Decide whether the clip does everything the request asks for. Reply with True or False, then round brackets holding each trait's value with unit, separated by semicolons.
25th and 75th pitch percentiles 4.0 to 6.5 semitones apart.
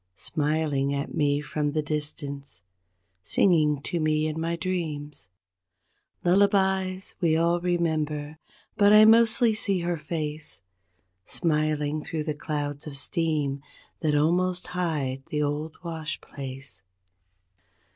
False (2.9 semitones)